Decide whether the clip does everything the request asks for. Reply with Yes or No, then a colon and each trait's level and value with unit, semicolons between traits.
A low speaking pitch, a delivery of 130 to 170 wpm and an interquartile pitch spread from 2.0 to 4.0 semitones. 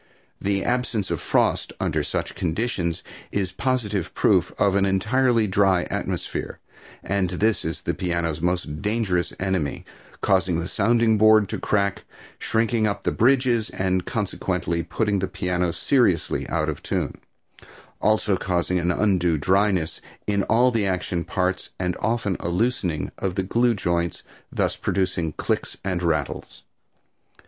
Yes: very low, 95 Hz; average, 140 wpm; average, 3.6 semitones